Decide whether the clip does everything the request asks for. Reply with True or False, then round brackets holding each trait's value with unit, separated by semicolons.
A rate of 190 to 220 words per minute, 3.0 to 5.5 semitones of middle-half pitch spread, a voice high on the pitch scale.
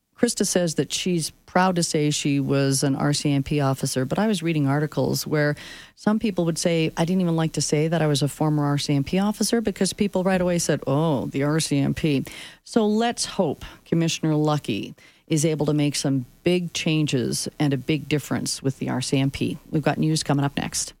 False (195 wpm; 3.6 semitones; 155 Hz)